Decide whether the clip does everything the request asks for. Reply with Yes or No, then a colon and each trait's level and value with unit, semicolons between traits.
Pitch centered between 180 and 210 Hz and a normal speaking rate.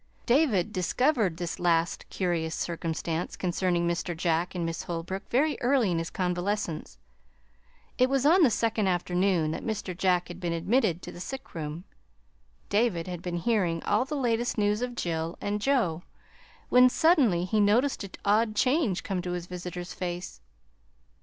Yes: medium, 185 Hz; average, 160 wpm